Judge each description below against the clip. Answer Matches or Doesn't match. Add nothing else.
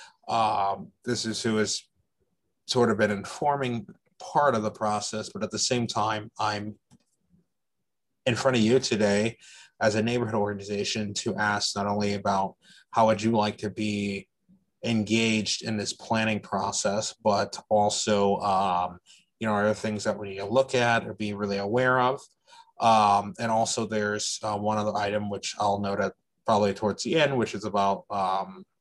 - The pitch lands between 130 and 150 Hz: Doesn't match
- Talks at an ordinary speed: Matches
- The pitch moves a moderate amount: Doesn't match